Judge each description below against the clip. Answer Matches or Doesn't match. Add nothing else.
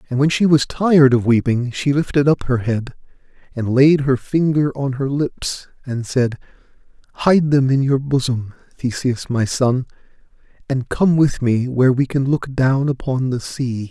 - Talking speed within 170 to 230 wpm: Matches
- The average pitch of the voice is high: Doesn't match